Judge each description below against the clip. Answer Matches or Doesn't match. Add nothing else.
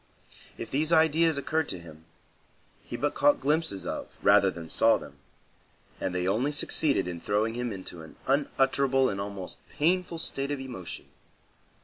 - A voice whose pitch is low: Matches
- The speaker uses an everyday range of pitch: Doesn't match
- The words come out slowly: Doesn't match